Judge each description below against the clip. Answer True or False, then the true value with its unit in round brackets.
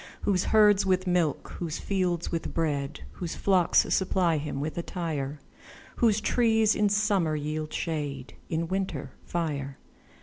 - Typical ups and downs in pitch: True (4.1 semitones)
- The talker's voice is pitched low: False (170 Hz)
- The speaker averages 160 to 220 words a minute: False (135 wpm)